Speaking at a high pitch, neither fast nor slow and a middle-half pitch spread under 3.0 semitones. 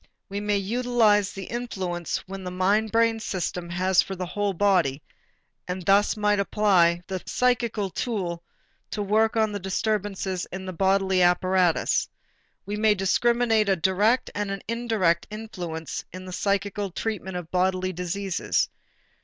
Yes: high, 195 Hz; average, 145 wpm; narrow, 2.5 semitones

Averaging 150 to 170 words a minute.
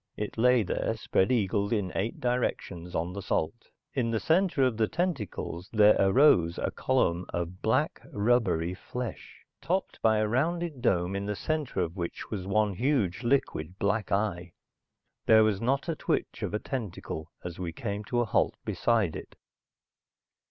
Yes: average, 165 wpm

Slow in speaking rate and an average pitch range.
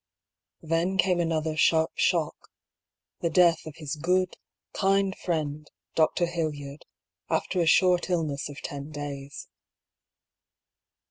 Yes: slow, 120 wpm; average, 3.1 semitones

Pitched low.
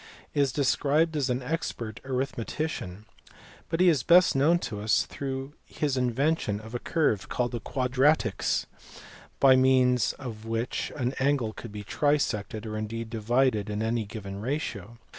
Yes: low, 125 Hz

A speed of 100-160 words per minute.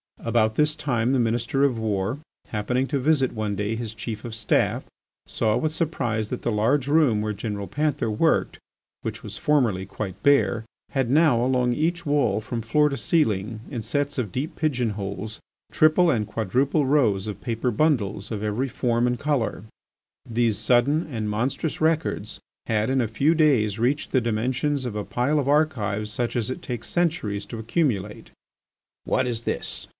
No: average, 175 wpm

